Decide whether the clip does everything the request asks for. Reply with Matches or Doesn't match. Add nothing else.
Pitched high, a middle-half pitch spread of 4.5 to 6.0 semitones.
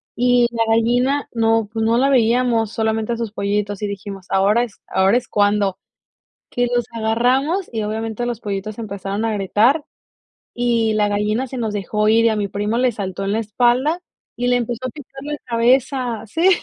Doesn't match